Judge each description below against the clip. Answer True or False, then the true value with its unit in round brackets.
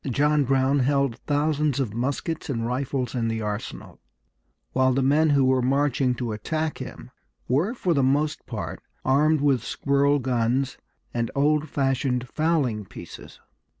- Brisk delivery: False (150 wpm)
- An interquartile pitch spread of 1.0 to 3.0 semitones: True (2.7 semitones)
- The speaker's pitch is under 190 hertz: True (135 Hz)